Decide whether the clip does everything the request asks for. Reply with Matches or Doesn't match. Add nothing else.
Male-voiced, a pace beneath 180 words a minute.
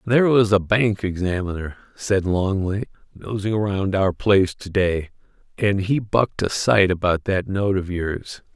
Matches